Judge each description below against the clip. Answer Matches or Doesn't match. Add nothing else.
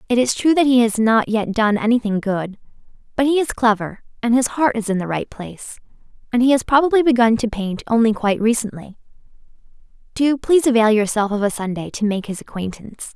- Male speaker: Doesn't match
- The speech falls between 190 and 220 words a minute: Matches